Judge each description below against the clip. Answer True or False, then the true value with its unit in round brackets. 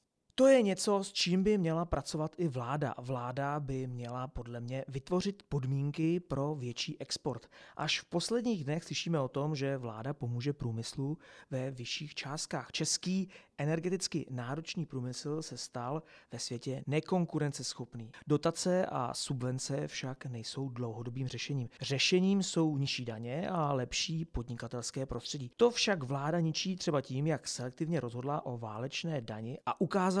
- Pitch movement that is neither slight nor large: True (4.7 semitones)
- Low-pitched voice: False (145 Hz)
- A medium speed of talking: True (145 wpm)